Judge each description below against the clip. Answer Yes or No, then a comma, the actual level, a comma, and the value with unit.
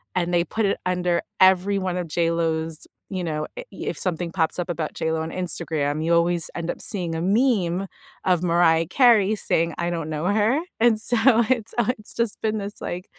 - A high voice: No, medium, 175 Hz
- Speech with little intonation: No, average, 3.5 semitones